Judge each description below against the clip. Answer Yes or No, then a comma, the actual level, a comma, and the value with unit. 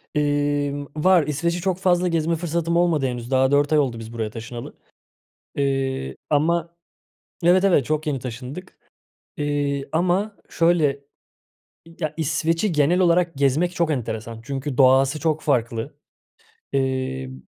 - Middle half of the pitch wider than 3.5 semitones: Yes, average, 4.2 semitones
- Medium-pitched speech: Yes, medium, 145 Hz